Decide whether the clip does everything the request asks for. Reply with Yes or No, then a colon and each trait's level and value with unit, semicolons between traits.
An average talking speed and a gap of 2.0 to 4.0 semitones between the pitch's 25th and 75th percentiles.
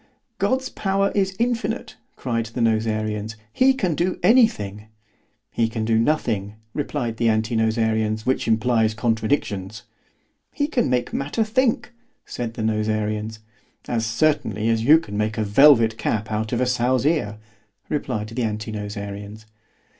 No: average, 145 wpm; average, 5.0 semitones